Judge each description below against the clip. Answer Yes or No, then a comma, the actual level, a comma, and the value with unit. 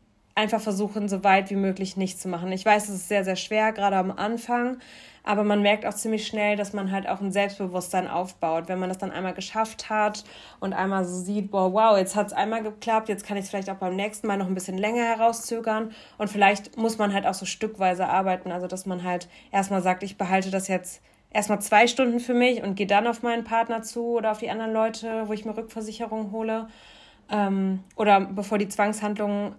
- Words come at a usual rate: No, fast, 220 wpm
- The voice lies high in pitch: Yes, high, 205 Hz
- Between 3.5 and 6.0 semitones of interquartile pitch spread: No, narrow, 2.5 semitones